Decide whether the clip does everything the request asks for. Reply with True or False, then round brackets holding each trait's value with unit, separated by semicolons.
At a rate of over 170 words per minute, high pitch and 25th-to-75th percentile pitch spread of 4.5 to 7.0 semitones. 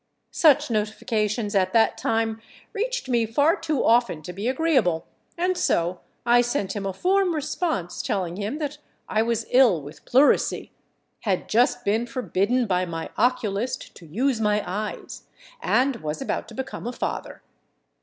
False (155 wpm; 225 Hz; 4.9 semitones)